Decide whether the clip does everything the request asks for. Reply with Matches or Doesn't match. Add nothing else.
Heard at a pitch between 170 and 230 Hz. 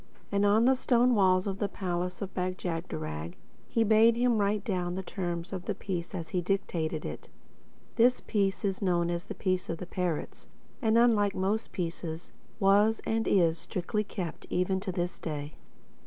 Matches